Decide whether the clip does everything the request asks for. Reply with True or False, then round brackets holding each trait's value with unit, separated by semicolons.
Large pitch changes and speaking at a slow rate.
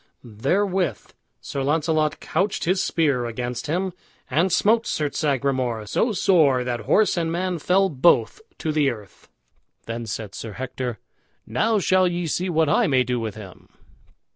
False (6.6 semitones; 155 wpm)